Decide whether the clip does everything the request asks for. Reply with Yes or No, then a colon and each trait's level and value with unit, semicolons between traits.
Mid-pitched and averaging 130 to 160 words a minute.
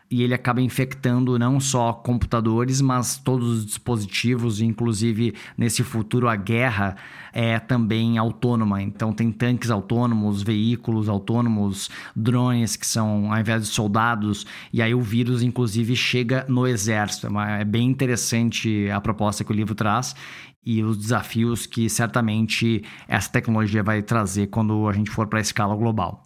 No: low, 115 Hz; average, 150 wpm